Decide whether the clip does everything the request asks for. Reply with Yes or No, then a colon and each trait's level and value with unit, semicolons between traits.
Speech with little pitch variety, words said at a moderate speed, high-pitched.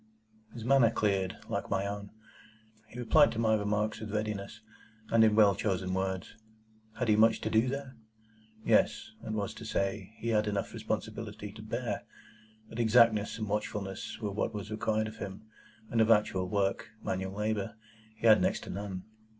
No: narrow, 1.9 semitones; average, 165 wpm; low, 110 Hz